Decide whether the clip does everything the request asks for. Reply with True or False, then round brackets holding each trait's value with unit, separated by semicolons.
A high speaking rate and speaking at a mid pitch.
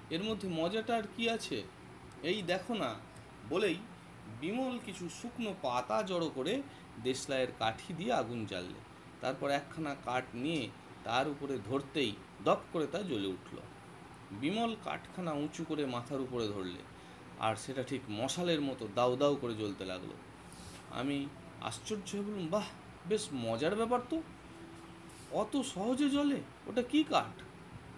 True (135 wpm; 145 Hz)